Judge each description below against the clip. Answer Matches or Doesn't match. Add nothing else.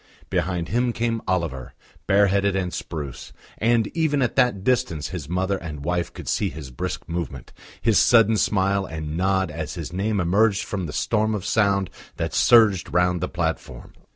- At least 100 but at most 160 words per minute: Doesn't match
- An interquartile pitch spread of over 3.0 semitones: Matches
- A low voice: Matches